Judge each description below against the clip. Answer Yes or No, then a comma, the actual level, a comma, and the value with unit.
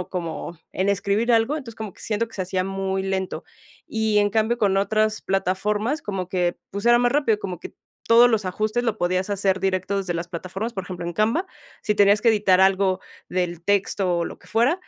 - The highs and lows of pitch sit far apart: No, average, 2.9 semitones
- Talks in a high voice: Yes, high, 200 Hz